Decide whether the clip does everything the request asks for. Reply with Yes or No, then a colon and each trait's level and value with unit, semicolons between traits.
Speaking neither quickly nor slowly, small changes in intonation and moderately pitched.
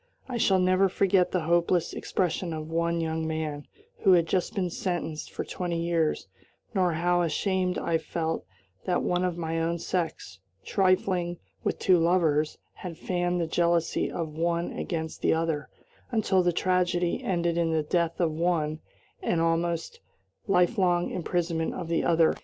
Yes: average, 160 wpm; narrow, 1.8 semitones; medium, 170 Hz